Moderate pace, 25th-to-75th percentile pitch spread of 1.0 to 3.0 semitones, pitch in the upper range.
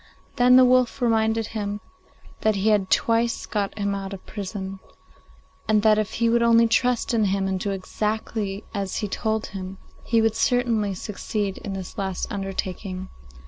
Yes: average, 170 wpm; narrow, 2.6 semitones; high, 210 Hz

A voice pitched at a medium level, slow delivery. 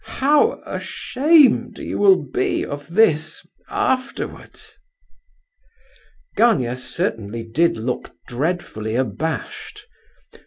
Yes: medium, 155 Hz; slow, 80 wpm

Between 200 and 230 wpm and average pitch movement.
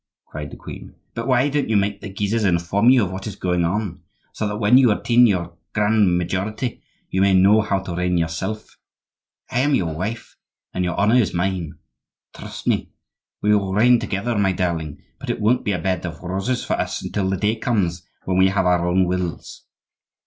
Yes: fast, 205 wpm; average, 3.4 semitones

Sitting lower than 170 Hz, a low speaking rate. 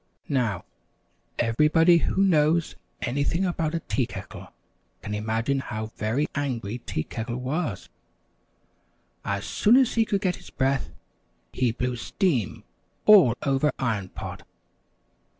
Yes: low, 135 Hz; slow, 125 wpm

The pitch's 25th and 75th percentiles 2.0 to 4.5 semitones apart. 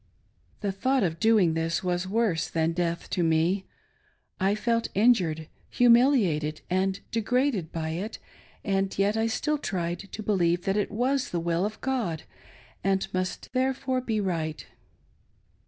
No: average, 5.1 semitones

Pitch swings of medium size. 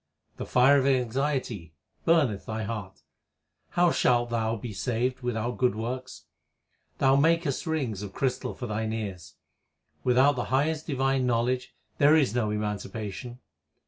Yes: average, 3.4 semitones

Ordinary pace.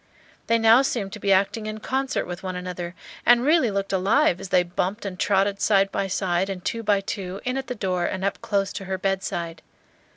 No: fast, 220 wpm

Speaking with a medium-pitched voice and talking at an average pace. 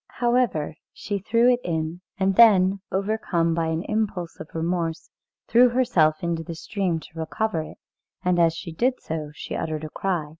Yes: medium, 175 Hz; average, 175 wpm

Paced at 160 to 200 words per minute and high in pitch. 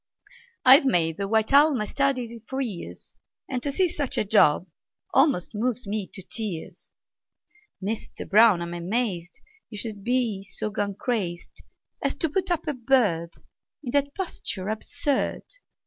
No: average, 150 wpm; high, 225 Hz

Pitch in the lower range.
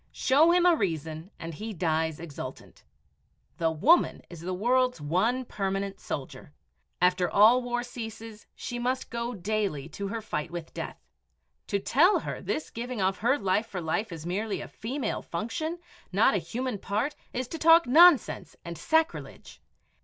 No: high, 215 Hz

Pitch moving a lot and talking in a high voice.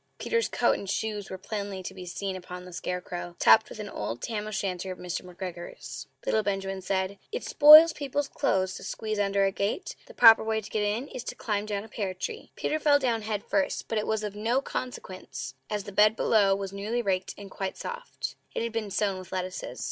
No: average, 2.9 semitones; high, 205 Hz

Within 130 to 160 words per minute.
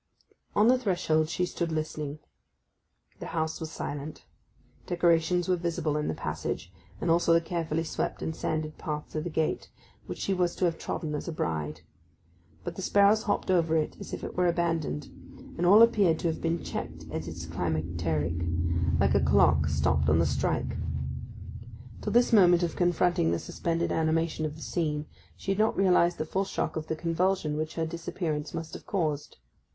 No: average, 185 wpm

